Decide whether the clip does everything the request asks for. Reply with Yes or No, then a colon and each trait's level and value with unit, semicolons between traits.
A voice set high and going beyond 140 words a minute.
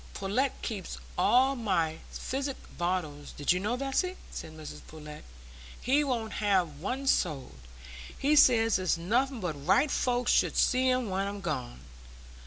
Yes: high, 205 Hz; average, 150 wpm